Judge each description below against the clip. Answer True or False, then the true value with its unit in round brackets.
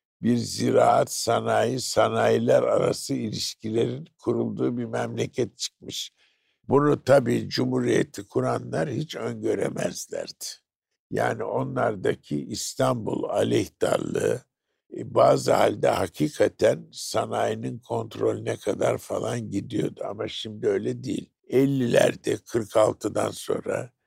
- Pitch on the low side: True (100 Hz)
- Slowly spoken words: True (85 wpm)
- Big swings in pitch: True (8.8 semitones)